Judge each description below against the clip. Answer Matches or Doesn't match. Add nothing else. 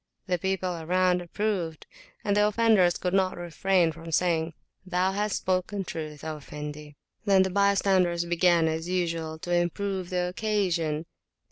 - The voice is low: Doesn't match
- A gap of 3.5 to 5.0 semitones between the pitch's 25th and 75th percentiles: Doesn't match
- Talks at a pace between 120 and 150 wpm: Matches